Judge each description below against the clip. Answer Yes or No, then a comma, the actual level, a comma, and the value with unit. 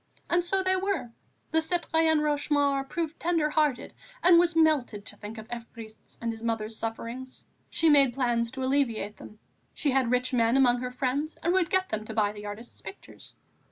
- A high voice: Yes, very high, 265 Hz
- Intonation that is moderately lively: No, wide, 5.7 semitones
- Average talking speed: Yes, average, 190 wpm